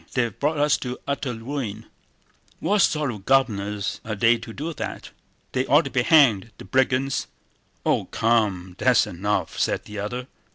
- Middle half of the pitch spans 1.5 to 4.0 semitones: No, average, 4.7 semitones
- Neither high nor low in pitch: No, low, 120 Hz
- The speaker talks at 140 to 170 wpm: Yes, average, 160 wpm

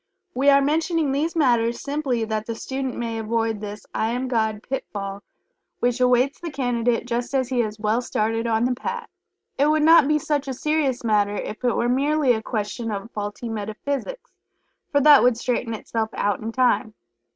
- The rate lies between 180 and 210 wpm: Yes, average, 185 wpm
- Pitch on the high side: Yes, high, 245 Hz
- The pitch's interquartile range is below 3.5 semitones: No, average, 3.9 semitones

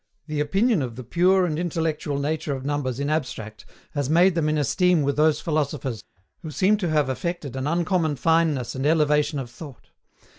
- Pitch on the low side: No, medium, 150 Hz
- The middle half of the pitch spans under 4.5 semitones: Yes, average, 3.1 semitones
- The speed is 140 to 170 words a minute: No, average, 185 wpm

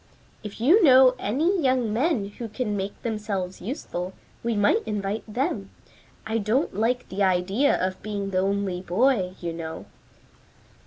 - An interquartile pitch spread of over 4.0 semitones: Yes, average, 4.6 semitones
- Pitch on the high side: Yes, high, 210 Hz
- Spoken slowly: No, average, 150 wpm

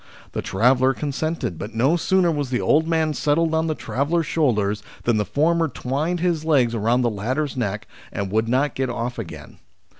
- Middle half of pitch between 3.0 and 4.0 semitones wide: No, wide, 5.4 semitones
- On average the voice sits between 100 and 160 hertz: Yes, low, 135 Hz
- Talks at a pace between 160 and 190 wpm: Yes, average, 185 wpm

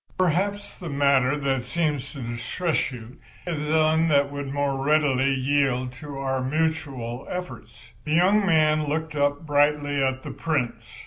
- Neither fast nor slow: Yes, average, 150 wpm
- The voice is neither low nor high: Yes, medium, 145 Hz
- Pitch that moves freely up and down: No, average, 2.8 semitones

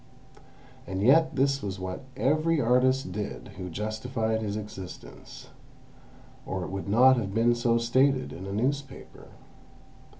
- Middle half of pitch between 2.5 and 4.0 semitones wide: No, average, 5.0 semitones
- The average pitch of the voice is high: No, low, 115 Hz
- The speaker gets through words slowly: Yes, slow, 130 wpm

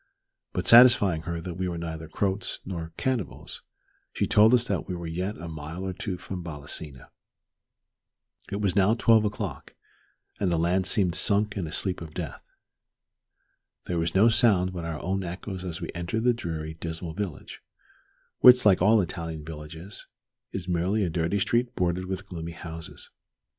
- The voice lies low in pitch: Yes, very low, 90 Hz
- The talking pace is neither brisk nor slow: Yes, average, 170 wpm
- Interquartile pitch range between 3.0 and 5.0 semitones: Yes, average, 3.6 semitones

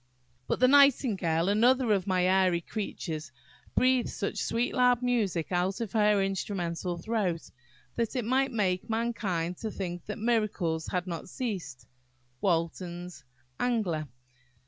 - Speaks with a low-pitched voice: No, high, 195 Hz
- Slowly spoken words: Yes, slow, 125 wpm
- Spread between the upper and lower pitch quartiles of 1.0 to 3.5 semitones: No, average, 5.1 semitones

